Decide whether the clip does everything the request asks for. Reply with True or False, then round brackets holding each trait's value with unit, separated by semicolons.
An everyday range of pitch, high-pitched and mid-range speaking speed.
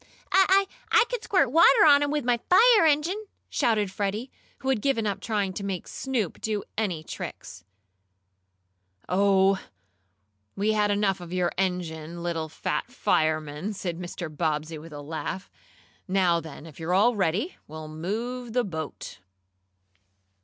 False (6.6 semitones; 195 Hz; 145 wpm)